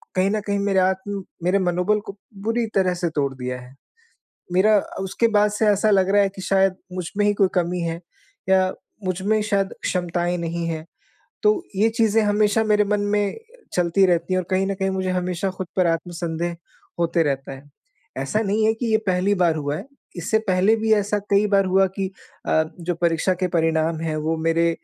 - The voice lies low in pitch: No, medium, 185 Hz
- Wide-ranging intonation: No, average, 3.2 semitones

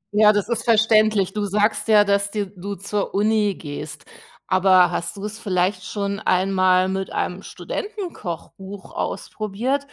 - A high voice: Yes, high, 200 Hz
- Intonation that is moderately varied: No, narrow, 2.3 semitones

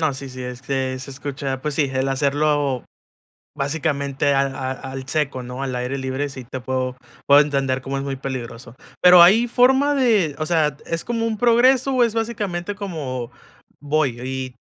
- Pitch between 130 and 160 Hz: Yes, medium, 140 Hz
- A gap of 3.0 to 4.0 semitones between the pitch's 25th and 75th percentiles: No, average, 4.7 semitones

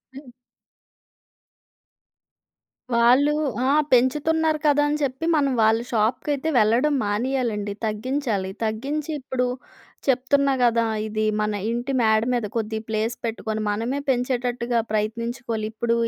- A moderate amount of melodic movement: Yes, average, 3.7 semitones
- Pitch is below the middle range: No, high, 240 Hz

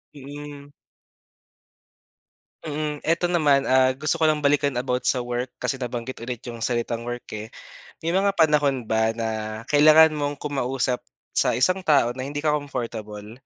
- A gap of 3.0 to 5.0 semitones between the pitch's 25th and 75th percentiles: Yes, average, 3.5 semitones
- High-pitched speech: No, low, 135 Hz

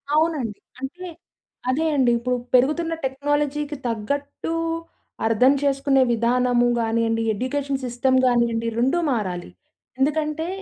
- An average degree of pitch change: Yes, average, 3.6 semitones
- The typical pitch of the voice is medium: No, very high, 265 Hz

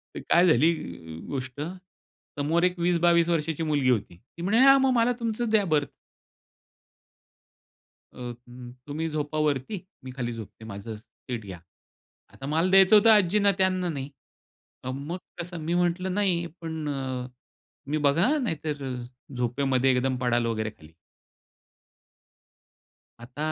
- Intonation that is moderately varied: No, wide, 5.8 semitones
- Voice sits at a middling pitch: Yes, medium, 150 Hz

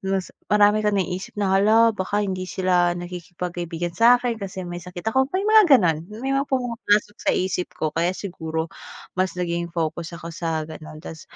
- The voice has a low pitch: No, medium, 185 Hz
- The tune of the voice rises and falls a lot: No, average, 3.8 semitones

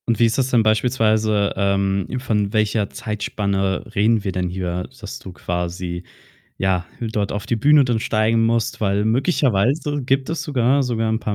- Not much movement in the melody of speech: No, average, 3.2 semitones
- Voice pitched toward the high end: No, low, 110 Hz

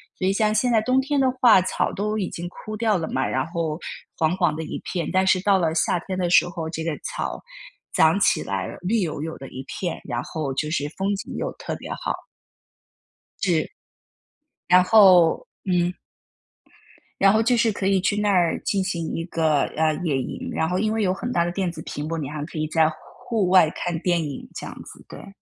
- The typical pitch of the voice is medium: Yes, medium, 180 Hz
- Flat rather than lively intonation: No, average, 3.9 semitones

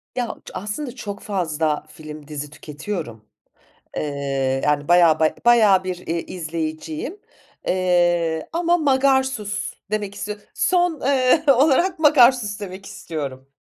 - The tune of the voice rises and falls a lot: Yes, wide, 8.0 semitones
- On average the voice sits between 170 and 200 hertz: Yes, medium, 185 Hz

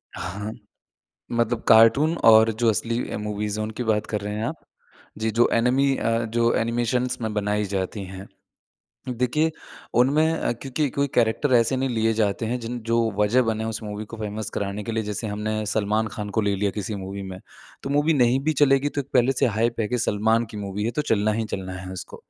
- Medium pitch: No, low, 110 Hz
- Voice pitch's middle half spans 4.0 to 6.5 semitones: No, average, 2.7 semitones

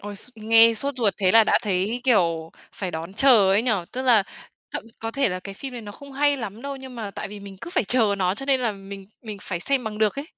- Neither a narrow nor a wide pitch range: Yes, average, 4.4 semitones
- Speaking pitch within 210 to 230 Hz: Yes, high, 220 Hz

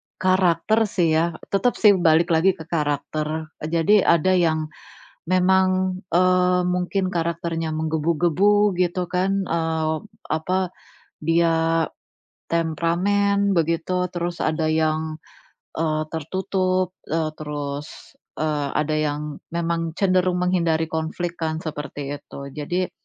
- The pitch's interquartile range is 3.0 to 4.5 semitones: No, narrow, 2.6 semitones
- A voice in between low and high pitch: Yes, medium, 170 Hz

